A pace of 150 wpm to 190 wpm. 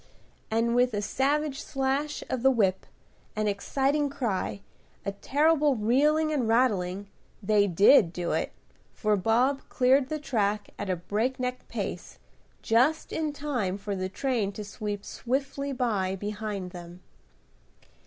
No: slow, 135 wpm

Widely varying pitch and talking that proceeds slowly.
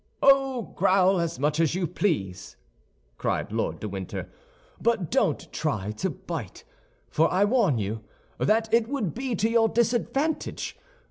No: wide, 7.5 semitones; average, 145 wpm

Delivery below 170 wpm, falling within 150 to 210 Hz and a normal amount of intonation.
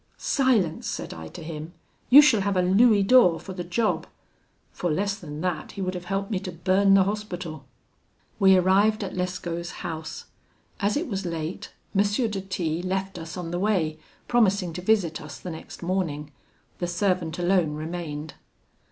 No: average, 175 wpm; medium, 185 Hz; average, 3.2 semitones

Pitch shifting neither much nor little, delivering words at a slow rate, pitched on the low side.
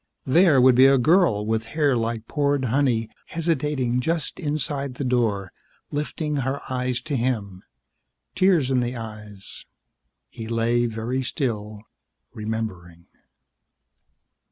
Yes: average, 4.1 semitones; slow, 120 wpm; low, 125 Hz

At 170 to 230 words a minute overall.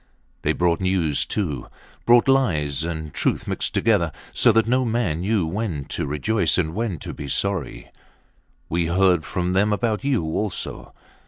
No: average, 160 wpm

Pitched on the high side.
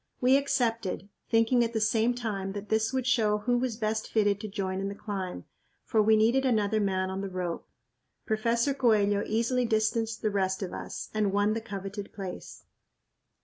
Yes: high, 215 Hz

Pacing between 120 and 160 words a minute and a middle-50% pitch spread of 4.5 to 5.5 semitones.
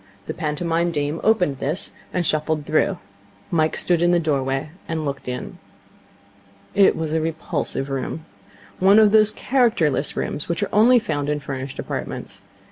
No: average, 155 wpm; average, 3.6 semitones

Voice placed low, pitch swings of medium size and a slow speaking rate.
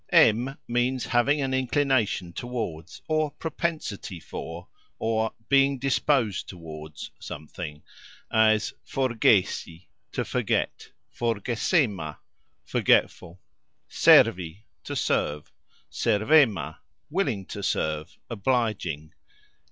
No: low, 110 Hz; wide, 7.0 semitones; slow, 90 wpm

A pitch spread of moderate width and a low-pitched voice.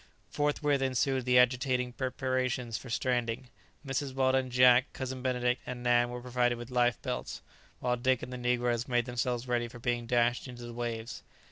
No: narrow, 1.2 semitones; low, 125 Hz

